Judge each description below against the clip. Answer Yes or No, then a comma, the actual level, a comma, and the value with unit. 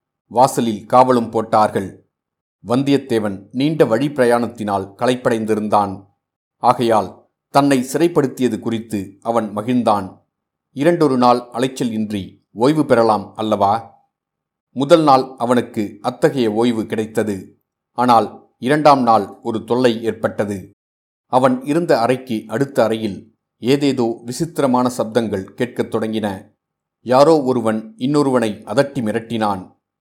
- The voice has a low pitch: Yes, low, 115 Hz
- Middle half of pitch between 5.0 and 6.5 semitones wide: No, average, 3.5 semitones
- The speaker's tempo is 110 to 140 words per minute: No, average, 95 wpm